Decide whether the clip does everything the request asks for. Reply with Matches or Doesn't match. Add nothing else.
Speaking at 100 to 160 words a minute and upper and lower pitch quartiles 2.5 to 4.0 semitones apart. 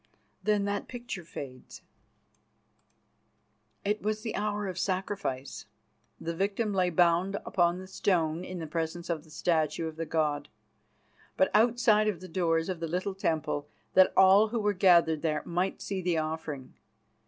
Matches